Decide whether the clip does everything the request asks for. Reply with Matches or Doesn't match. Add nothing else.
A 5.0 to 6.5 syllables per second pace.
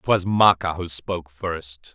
Doesn't match